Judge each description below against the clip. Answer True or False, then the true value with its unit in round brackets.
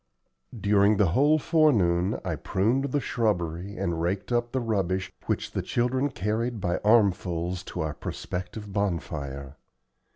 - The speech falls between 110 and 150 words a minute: True (135 wpm)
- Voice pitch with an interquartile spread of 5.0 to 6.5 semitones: True (5.3 semitones)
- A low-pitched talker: True (100 Hz)